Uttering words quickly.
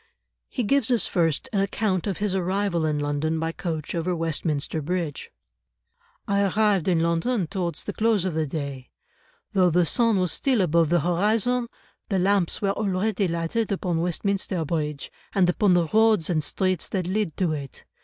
No: average, 175 wpm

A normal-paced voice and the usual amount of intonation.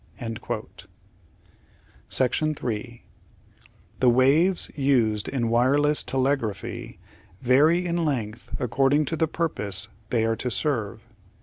No: slow, 100 wpm; average, 4.3 semitones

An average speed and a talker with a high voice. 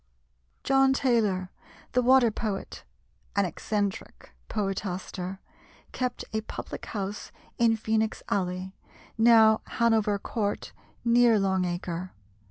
No: slow, 100 wpm; high, 210 Hz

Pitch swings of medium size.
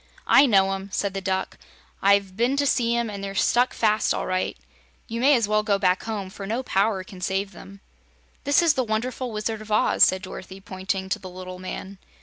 Yes: average, 3.3 semitones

